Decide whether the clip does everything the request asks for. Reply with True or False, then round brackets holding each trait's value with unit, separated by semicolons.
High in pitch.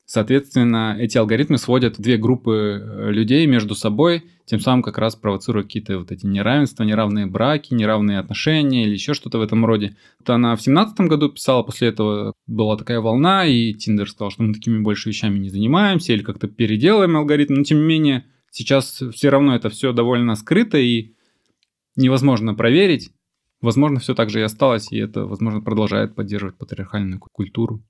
False (115 Hz)